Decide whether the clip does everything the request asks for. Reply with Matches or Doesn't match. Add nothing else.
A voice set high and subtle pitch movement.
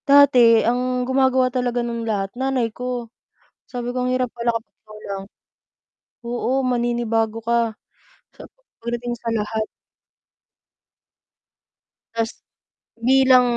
Matches